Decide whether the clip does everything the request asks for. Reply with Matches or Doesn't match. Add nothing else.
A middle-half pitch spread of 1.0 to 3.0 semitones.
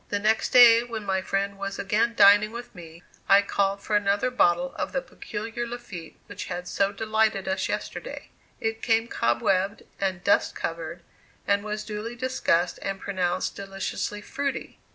Matches